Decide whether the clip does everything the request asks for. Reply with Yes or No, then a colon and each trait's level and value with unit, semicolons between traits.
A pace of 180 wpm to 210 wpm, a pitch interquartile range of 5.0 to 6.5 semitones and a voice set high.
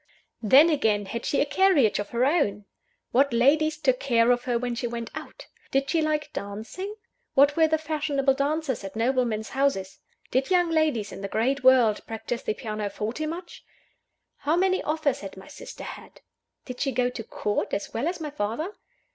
Yes: average, 185 wpm; wide, 5.4 semitones; very high, 265 Hz